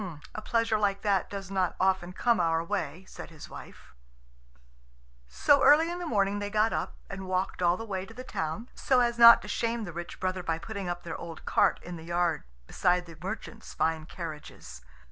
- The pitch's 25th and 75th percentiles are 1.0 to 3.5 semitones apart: No, average, 4.2 semitones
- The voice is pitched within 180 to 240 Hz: Yes, high, 190 Hz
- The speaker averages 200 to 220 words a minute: Yes, fast, 205 wpm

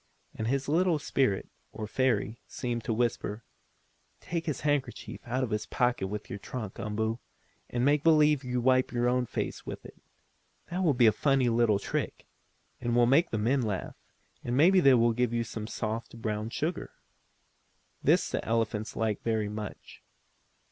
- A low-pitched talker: Yes, low, 120 Hz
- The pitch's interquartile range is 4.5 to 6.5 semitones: No, average, 3.4 semitones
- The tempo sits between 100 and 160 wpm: No, average, 170 wpm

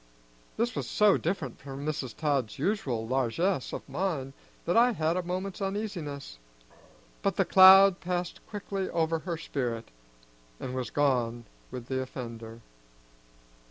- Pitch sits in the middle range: Yes, medium, 155 Hz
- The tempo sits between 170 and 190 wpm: No, slow, 135 wpm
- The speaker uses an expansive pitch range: Yes, wide, 6.7 semitones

